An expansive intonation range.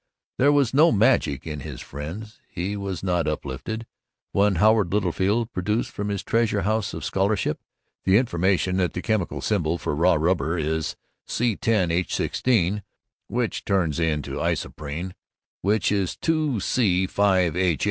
No: average, 4.2 semitones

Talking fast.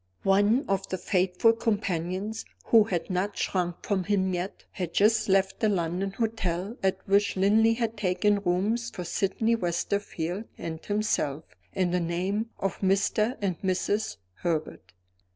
No: average, 145 wpm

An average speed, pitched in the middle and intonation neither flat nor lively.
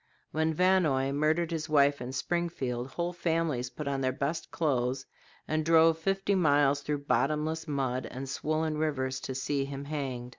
Yes: average, 160 wpm; medium, 145 Hz; average, 3.2 semitones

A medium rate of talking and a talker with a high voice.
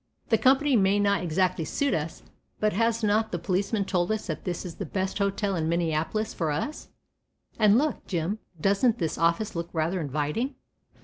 Yes: average, 180 wpm; high, 195 Hz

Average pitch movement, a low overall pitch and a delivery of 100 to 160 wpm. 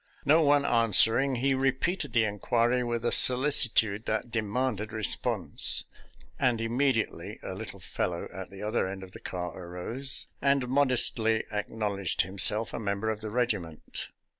Yes: average, 4.0 semitones; low, 115 Hz; average, 155 wpm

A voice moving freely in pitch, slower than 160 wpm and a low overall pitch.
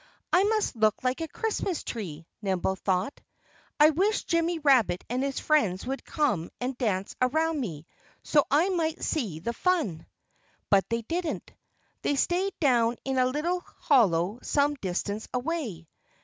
No: wide, 7.8 semitones; average, 150 wpm; very high, 260 Hz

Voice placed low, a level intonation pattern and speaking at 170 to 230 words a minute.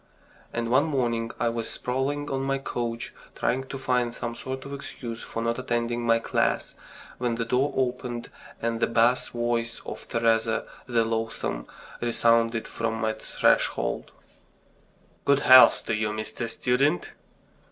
No: low, 120 Hz; narrow, 1.9 semitones; average, 145 wpm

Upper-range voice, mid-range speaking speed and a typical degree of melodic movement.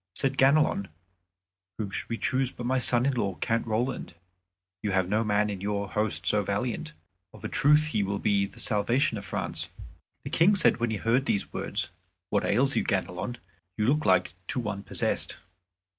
No: low, 110 Hz; average, 190 wpm; average, 4.3 semitones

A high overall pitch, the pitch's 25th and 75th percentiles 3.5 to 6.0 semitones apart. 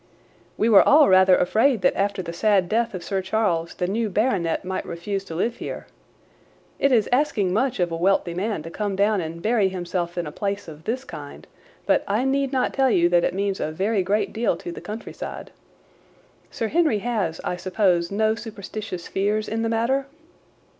Yes: high, 200 Hz; average, 4.0 semitones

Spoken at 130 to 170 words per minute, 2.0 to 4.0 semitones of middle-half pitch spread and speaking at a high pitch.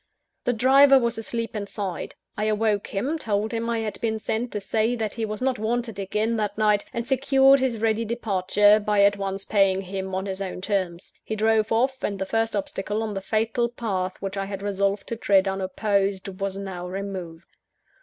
No: average, 195 wpm; narrow, 2.6 semitones; high, 210 Hz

